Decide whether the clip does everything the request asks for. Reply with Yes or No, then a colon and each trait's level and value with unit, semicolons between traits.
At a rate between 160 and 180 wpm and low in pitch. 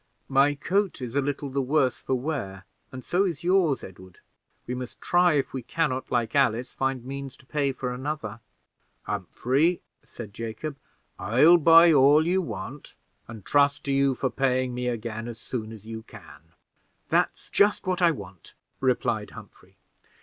Yes: average, 170 wpm; low, 130 Hz